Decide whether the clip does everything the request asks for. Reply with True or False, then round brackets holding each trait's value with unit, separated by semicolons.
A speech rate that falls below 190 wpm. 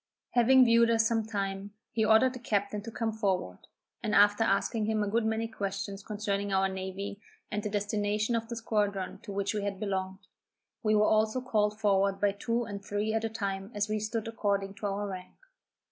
False (200 wpm)